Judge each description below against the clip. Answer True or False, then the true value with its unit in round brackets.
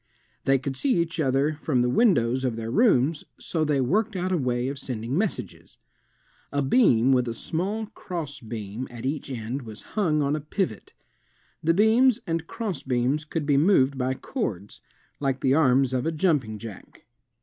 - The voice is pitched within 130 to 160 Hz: True (140 Hz)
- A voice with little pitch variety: False (5.1 semitones)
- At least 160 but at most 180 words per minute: True (170 wpm)